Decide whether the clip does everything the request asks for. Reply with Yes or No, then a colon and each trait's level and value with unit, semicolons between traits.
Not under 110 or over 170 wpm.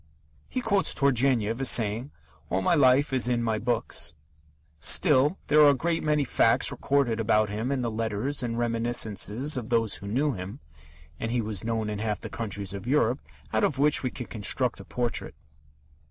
No: average, 185 wpm